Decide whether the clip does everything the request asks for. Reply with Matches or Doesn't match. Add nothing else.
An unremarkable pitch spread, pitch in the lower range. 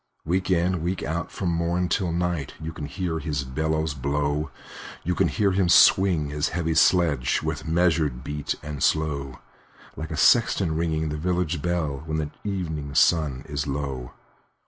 Matches